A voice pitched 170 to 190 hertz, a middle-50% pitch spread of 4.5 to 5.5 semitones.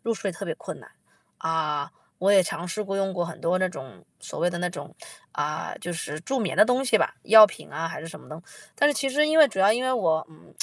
Yes: medium, 185 Hz; average, 5.0 semitones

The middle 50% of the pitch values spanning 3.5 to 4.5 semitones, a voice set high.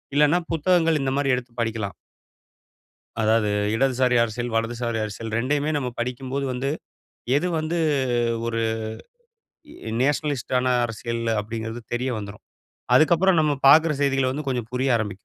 No: average, 4.1 semitones; low, 125 Hz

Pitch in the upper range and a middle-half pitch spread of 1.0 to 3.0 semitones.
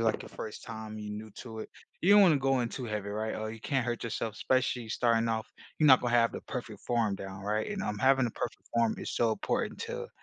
No: low, 115 Hz; narrow, 2.6 semitones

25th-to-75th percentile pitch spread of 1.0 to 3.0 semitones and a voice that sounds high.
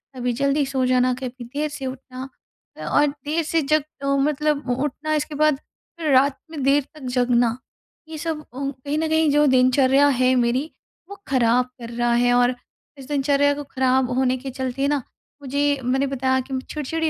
Yes: narrow, 2.6 semitones; very high, 270 Hz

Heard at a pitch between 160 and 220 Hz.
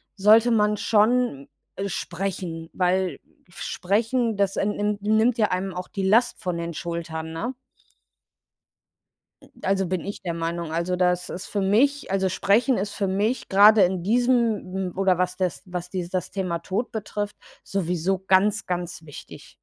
Yes: high, 190 Hz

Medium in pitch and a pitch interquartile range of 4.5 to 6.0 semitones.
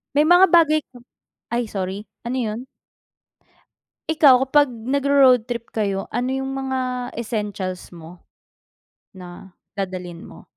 No: high, 240 Hz; average, 5.2 semitones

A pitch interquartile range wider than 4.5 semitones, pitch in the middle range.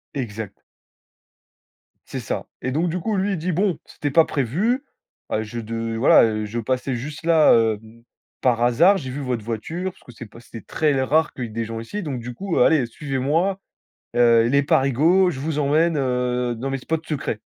No: wide, 5.5 semitones; low, 130 Hz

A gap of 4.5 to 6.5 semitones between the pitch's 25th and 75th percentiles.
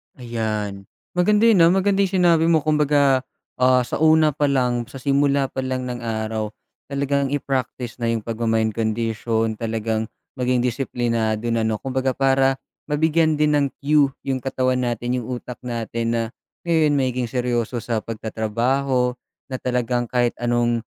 No: average, 3.3 semitones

